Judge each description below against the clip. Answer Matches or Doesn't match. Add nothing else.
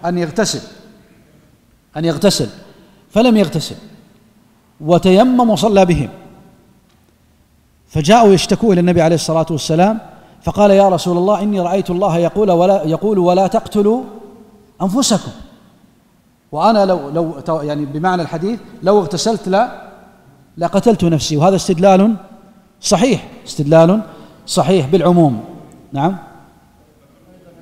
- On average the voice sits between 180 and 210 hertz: Matches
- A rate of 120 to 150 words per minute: Doesn't match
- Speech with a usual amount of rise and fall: Matches